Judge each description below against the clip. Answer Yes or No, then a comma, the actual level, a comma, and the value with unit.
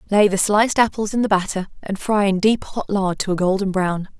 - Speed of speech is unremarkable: No, fast, 245 wpm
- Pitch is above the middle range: Yes, high, 200 Hz